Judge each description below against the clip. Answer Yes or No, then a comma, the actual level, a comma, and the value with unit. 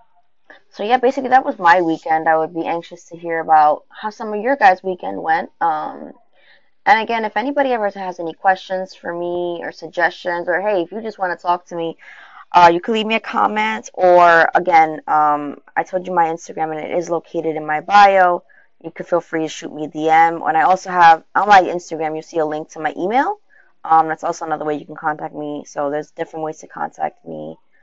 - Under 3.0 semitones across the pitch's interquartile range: No, average, 3.9 semitones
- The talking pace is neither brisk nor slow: No, fast, 225 wpm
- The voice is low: No, medium, 170 Hz